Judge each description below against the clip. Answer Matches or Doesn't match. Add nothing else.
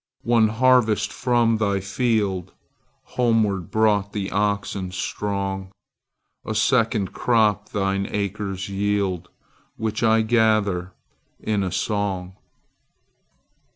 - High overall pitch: Doesn't match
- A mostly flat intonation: Matches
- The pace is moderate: Doesn't match